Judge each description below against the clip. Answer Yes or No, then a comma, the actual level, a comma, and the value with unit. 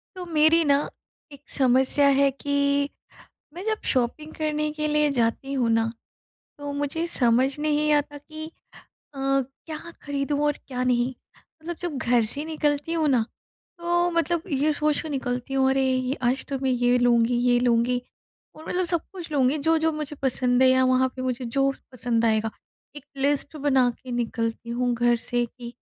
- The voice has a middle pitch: No, very high, 275 Hz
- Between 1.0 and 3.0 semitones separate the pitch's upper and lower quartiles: No, average, 3.4 semitones